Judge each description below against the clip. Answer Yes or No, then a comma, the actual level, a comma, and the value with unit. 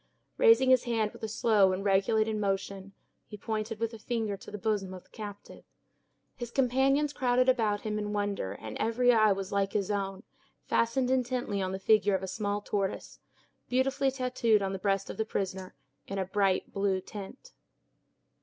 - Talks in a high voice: Yes, high, 210 Hz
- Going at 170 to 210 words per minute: Yes, average, 180 wpm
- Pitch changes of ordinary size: Yes, average, 3.4 semitones